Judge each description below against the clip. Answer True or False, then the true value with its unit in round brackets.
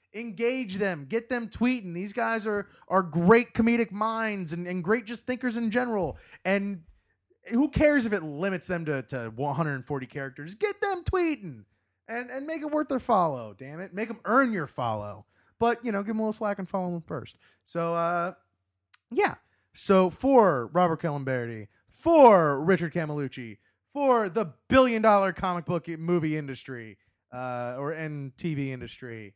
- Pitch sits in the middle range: True (180 Hz)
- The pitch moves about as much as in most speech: False (8.7 semitones)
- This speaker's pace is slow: False (170 wpm)